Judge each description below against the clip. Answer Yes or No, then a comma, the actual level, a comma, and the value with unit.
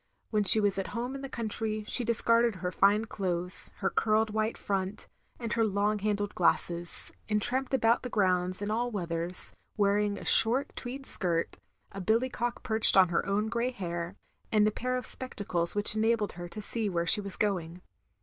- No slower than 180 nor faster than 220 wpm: Yes, average, 190 wpm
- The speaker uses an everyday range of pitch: Yes, average, 3.6 semitones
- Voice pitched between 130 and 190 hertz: No, high, 210 Hz